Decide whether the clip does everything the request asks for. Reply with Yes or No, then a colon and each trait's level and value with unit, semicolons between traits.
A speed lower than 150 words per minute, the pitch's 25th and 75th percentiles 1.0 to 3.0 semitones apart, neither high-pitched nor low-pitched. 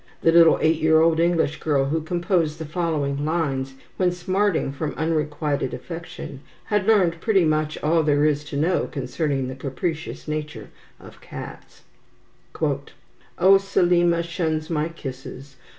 Yes: average, 140 wpm; average, 2.7 semitones; medium, 160 Hz